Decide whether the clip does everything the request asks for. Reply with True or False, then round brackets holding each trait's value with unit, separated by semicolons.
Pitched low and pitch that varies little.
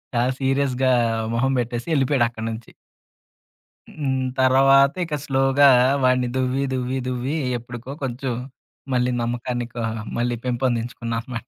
True (125 Hz; 1.8 semitones)